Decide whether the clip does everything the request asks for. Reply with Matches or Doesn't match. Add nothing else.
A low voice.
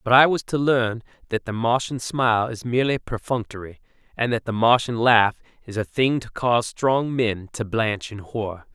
Matches